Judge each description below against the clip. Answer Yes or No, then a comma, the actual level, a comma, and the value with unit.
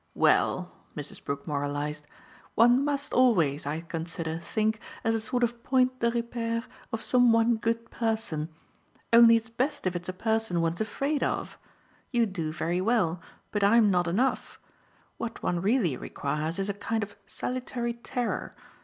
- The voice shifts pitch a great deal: Yes, wide, 5.7 semitones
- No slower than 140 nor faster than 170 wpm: Yes, average, 160 wpm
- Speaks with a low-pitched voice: No, high, 220 Hz